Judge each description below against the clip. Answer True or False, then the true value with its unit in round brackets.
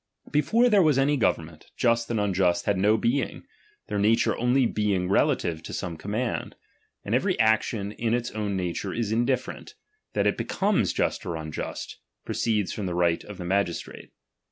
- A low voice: True (105 Hz)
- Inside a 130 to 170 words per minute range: False (195 wpm)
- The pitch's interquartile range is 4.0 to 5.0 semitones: True (4.6 semitones)